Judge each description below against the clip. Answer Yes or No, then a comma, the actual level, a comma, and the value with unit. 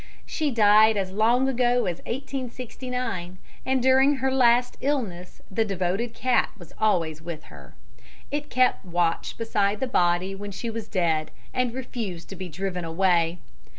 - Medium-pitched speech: No, high, 215 Hz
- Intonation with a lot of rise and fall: Yes, wide, 6.0 semitones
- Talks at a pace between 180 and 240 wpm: No, average, 150 wpm